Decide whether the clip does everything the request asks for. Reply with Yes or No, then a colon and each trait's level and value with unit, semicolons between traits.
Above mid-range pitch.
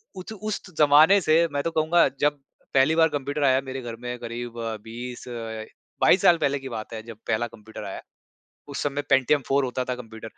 No: low, 135 Hz